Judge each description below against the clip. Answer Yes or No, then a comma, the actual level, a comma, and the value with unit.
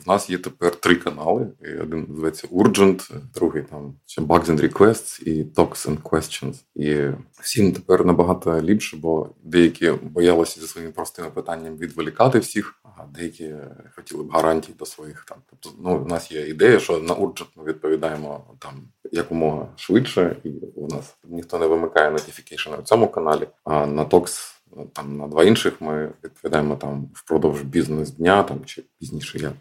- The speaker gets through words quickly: Yes, fast, 165 wpm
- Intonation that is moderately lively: No, narrow, 1.9 semitones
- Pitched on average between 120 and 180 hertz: No, very low, 80 Hz